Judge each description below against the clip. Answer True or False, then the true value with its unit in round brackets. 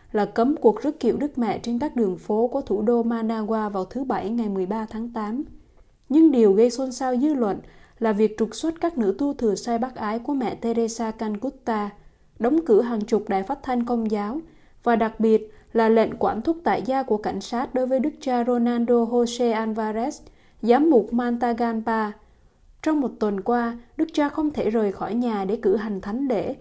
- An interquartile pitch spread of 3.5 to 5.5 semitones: False (3.0 semitones)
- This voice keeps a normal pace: True (205 wpm)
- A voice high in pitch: True (235 Hz)